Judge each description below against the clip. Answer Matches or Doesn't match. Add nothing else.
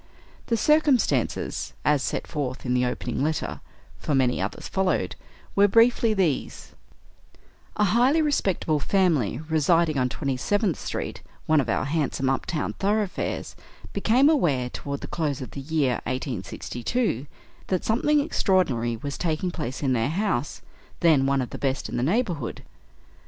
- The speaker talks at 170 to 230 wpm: Doesn't match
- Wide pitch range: Matches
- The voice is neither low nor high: Matches